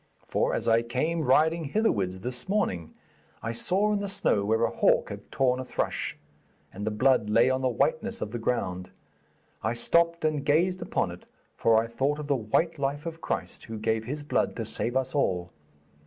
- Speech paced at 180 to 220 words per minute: Yes, average, 200 wpm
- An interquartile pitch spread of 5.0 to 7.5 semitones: Yes, wide, 5.6 semitones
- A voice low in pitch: Yes, low, 130 Hz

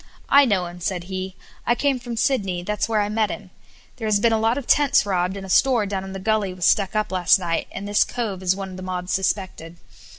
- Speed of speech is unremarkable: No, fast, 255 wpm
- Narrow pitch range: No, average, 3.1 semitones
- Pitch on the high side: Yes, high, 195 Hz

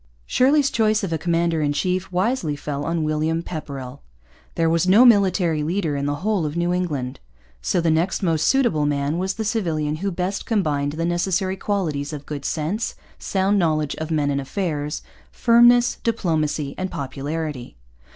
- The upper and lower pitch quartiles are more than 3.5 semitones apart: Yes, average, 4.4 semitones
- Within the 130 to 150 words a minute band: No, average, 170 wpm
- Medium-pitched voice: Yes, medium, 165 Hz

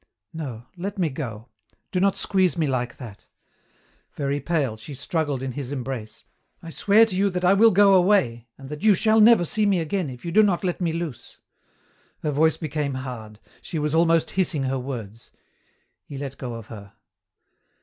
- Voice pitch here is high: No, medium, 150 Hz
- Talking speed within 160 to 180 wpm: No, average, 190 wpm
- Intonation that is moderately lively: No, wide, 6.1 semitones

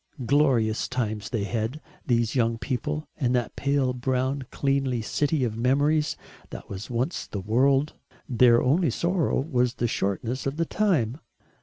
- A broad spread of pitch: No, average, 3.5 semitones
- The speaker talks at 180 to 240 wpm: No, average, 150 wpm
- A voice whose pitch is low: Yes, low, 125 Hz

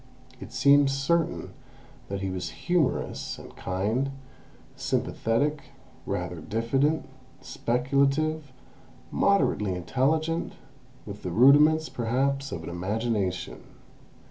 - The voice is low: Yes, low, 130 Hz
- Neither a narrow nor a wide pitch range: No, wide, 6.5 semitones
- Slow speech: Yes, slow, 90 wpm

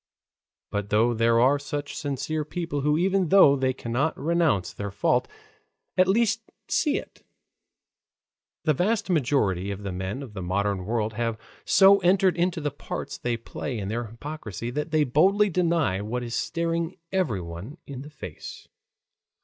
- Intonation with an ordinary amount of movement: No, wide, 7.3 semitones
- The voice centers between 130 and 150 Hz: Yes, medium, 140 Hz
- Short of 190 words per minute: Yes, average, 155 wpm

